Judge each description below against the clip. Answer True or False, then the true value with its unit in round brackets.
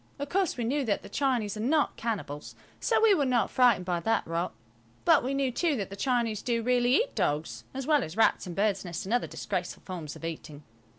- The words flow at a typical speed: False (230 wpm)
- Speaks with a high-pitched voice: True (230 Hz)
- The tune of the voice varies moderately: False (6.4 semitones)